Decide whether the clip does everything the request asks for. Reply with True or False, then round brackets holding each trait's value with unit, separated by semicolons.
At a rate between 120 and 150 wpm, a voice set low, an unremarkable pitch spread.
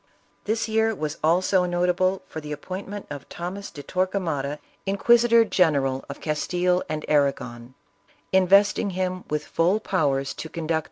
False (135 wpm; 180 Hz; 4.3 semitones)